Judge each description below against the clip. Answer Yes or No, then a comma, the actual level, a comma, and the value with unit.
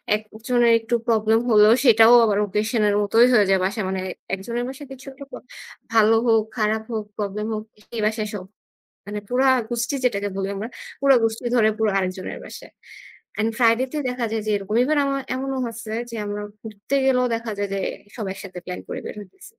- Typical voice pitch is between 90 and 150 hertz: No, high, 220 Hz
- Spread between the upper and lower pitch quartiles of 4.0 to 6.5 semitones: No, narrow, 2.5 semitones